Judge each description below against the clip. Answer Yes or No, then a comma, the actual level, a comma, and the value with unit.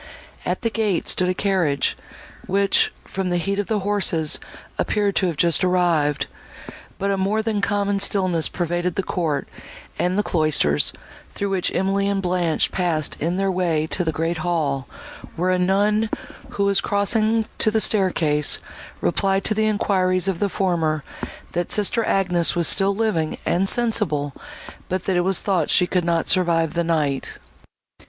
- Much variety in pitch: No, average, 3.2 semitones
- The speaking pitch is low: No, medium, 185 Hz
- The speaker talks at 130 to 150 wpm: No, average, 165 wpm